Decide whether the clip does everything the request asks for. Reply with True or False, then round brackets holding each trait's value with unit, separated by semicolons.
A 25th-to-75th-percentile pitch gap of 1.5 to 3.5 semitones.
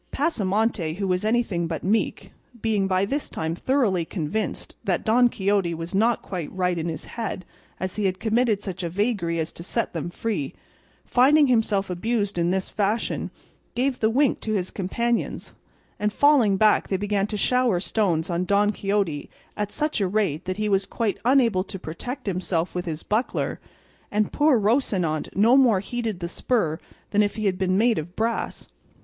False (4.0 semitones)